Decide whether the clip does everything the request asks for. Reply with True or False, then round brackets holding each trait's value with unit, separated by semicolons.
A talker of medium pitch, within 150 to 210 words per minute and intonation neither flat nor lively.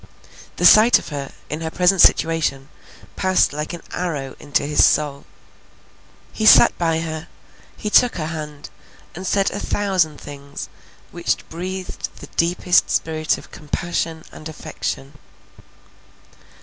False (160 Hz; 135 wpm; 3.2 semitones)